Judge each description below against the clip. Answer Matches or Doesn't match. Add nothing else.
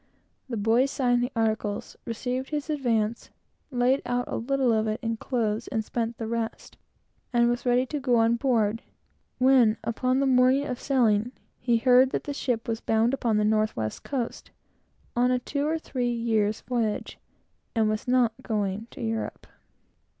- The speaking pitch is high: Matches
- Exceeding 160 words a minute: Matches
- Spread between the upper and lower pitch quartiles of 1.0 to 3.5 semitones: Matches